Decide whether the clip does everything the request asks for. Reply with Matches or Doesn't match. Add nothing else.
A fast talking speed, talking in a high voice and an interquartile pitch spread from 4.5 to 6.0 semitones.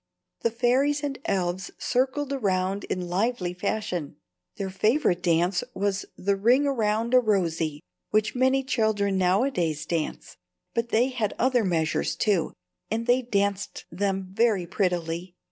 Doesn't match